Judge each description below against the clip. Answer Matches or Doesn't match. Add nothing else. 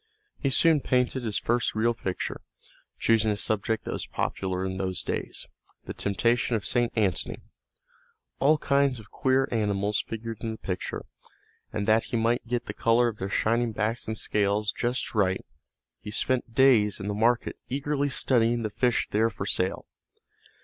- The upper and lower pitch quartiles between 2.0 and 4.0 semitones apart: Matches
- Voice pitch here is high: Doesn't match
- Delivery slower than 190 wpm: Matches